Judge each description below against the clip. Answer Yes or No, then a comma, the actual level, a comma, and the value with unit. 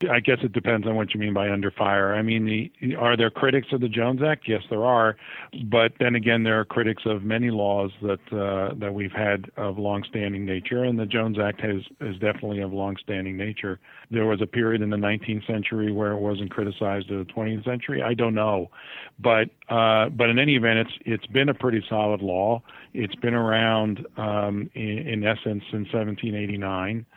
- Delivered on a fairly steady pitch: Yes, narrow, 2.2 semitones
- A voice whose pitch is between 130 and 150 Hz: No, low, 110 Hz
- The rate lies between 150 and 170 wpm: No, fast, 205 wpm